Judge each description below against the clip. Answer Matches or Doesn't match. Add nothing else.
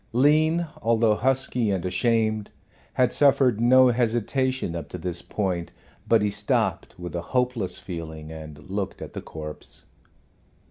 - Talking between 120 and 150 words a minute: Matches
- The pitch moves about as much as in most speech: Doesn't match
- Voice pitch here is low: Matches